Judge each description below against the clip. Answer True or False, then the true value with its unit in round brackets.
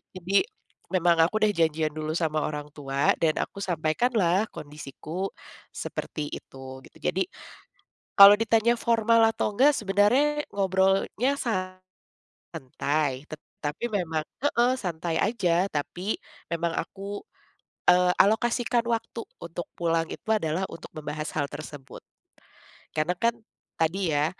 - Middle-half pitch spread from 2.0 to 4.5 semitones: False (5.4 semitones)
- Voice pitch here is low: False (175 Hz)